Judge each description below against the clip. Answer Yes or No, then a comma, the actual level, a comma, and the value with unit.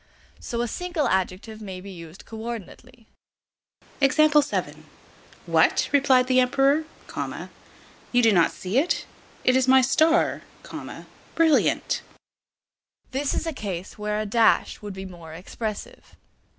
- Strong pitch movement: Yes, wide, 5.7 semitones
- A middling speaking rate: No, slow, 125 wpm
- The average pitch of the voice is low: No, high, 230 Hz